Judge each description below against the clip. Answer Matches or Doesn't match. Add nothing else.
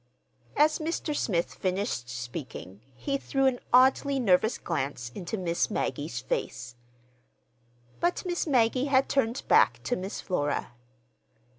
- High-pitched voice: Matches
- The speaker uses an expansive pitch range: Matches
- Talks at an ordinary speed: Doesn't match